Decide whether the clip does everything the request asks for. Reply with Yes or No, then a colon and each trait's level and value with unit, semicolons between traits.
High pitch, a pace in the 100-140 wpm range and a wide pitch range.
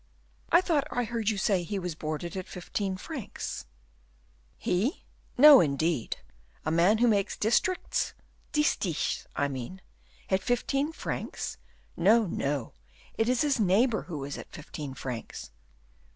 Yes: high, 195 Hz; slow, 135 wpm; wide, 7.1 semitones